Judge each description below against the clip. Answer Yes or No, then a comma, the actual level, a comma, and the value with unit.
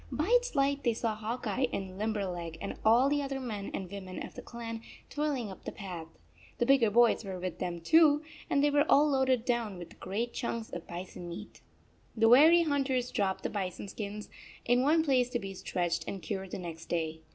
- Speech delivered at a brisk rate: Yes, fast, 210 wpm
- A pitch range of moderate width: No, wide, 6.0 semitones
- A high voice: Yes, high, 225 Hz